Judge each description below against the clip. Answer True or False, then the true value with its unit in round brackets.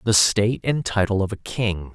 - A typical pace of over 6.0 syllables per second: False (4.9 syllables/s)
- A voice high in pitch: False (105 Hz)